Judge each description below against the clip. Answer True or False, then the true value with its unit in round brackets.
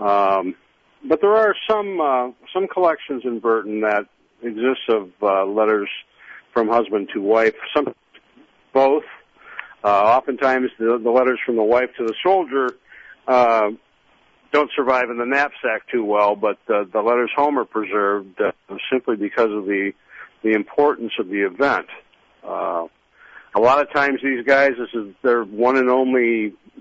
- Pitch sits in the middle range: False (120 Hz)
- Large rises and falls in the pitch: False (4.2 semitones)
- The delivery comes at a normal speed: True (155 wpm)